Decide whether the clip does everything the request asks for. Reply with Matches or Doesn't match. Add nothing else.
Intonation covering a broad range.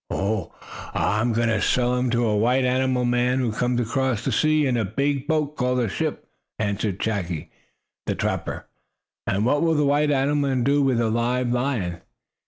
Doesn't match